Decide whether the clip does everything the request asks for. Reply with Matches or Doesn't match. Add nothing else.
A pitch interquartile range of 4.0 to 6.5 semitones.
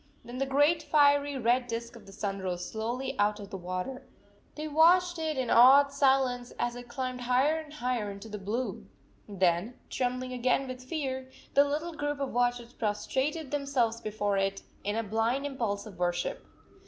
Matches